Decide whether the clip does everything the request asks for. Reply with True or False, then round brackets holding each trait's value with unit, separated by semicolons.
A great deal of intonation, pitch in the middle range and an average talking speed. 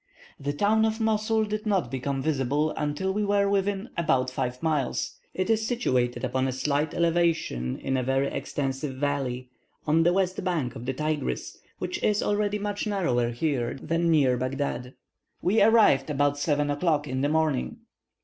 True (6.8 semitones; 150 Hz; 170 wpm)